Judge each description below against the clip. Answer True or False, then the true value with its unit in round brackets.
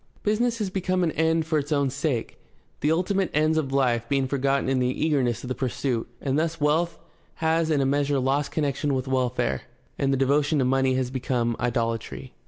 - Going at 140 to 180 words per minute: False (195 wpm)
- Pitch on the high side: False (140 Hz)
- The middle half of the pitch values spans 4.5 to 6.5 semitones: False (3.5 semitones)